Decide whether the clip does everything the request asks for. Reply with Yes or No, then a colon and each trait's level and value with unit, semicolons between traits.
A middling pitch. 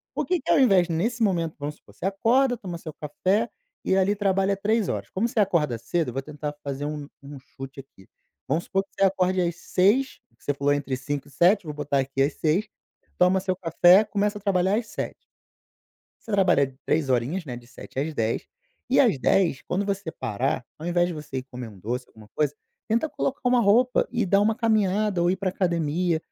Yes: medium, 175 Hz